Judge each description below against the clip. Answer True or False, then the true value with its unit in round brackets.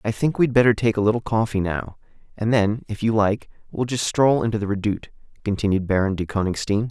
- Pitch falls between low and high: False (110 Hz)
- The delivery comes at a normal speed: False (210 wpm)